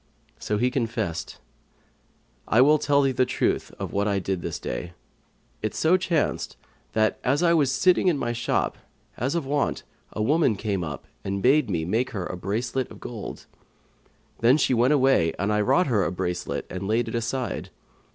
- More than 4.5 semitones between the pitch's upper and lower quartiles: Yes, wide, 5.5 semitones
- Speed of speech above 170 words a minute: Yes, average, 190 wpm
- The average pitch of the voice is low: Yes, low, 120 Hz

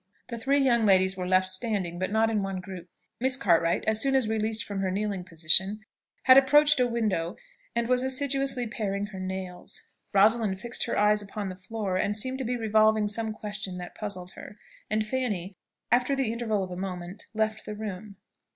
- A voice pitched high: Yes, high, 210 Hz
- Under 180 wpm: No, average, 195 wpm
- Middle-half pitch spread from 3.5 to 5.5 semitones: Yes, average, 3.8 semitones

